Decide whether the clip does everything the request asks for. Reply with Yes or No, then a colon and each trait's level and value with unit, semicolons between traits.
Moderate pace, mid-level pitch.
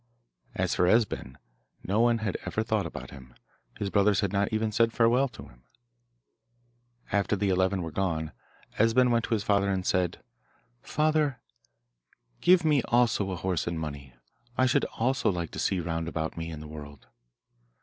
No: average, 170 wpm; low, 100 Hz